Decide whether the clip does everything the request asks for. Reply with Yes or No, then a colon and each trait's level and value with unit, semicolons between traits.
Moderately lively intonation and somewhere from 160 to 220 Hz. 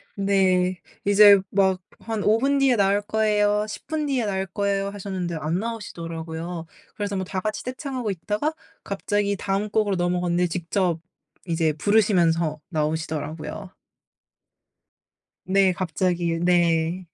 Yes: average, 3.3 semitones; high, 190 Hz